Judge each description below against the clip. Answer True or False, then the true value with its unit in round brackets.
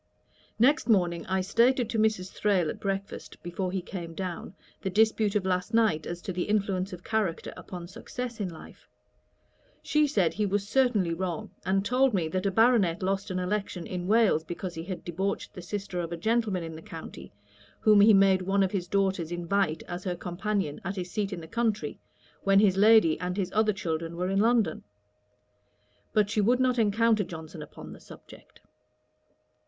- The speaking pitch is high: True (195 Hz)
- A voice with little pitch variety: False (3.3 semitones)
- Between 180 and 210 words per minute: True (190 wpm)